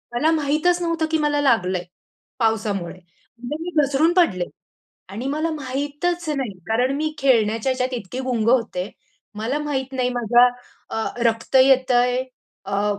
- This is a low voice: No, very high, 255 Hz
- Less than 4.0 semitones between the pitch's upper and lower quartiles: No, average, 4.8 semitones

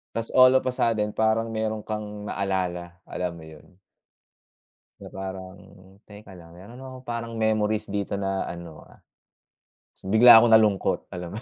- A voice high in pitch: No, low, 105 Hz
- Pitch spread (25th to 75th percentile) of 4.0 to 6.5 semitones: No, average, 3.1 semitones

